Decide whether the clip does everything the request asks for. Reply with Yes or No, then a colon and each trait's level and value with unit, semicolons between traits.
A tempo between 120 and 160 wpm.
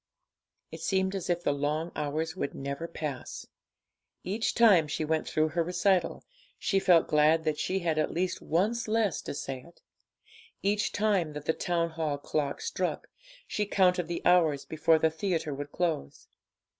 No: average, 170 wpm